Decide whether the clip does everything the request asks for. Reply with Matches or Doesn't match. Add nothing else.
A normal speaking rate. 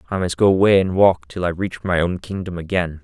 Doesn't match